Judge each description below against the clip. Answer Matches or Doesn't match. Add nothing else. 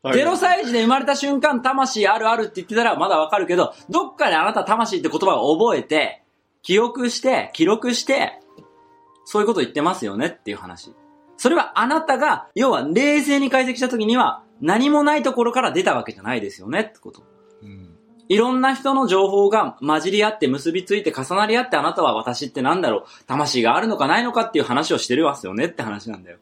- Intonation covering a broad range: Matches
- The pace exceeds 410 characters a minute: Matches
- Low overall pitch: Doesn't match